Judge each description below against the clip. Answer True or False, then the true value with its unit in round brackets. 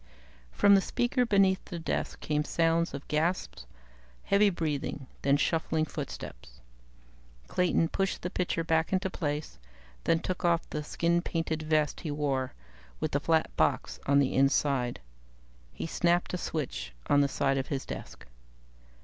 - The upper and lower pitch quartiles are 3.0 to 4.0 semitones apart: True (3.5 semitones)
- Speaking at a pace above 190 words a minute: False (155 wpm)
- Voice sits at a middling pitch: True (160 Hz)